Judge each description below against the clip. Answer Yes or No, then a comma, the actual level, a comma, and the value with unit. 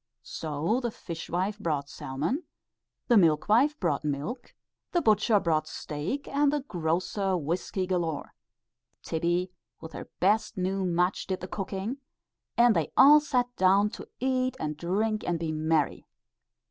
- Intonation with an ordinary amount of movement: No, wide, 5.8 semitones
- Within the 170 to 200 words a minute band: No, average, 145 wpm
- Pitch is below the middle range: No, medium, 185 Hz